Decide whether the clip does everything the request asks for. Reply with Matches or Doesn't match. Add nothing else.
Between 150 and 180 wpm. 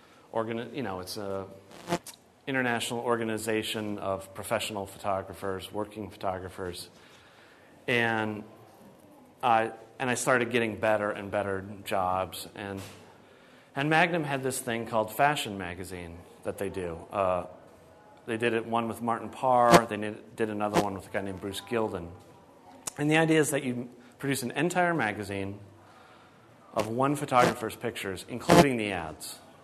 Doesn't match